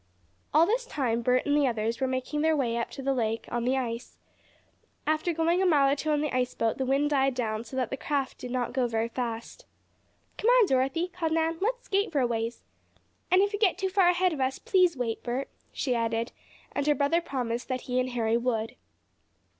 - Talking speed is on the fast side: Yes, fast, 225 wpm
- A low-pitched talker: No, very high, 265 Hz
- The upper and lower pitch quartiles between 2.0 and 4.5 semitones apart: No, average, 5.2 semitones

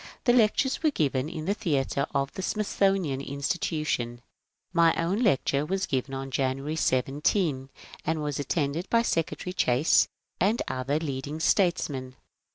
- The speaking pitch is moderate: Yes, medium, 150 Hz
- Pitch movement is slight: No, average, 5.2 semitones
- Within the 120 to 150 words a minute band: Yes, average, 145 wpm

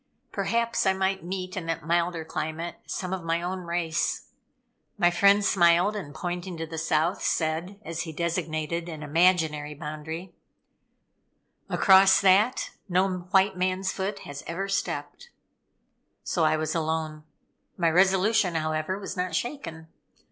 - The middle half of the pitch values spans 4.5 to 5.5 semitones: No, average, 2.9 semitones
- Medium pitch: Yes, medium, 175 Hz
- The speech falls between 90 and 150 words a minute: Yes, average, 140 wpm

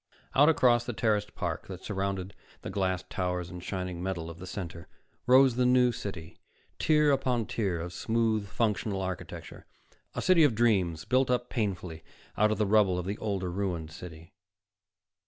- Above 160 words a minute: Yes, average, 170 wpm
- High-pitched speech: No, low, 100 Hz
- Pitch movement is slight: No, average, 4.6 semitones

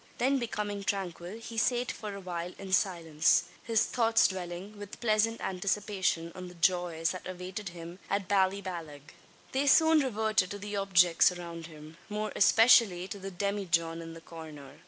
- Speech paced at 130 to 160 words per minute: Yes, average, 155 wpm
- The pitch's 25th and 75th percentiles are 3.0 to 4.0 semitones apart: Yes, average, 3.4 semitones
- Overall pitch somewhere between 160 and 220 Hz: Yes, high, 190 Hz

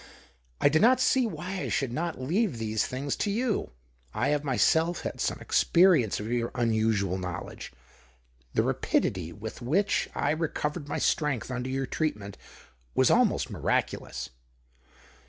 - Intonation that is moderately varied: No, wide, 7.4 semitones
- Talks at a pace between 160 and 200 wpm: No, average, 145 wpm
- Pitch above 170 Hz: No, low, 135 Hz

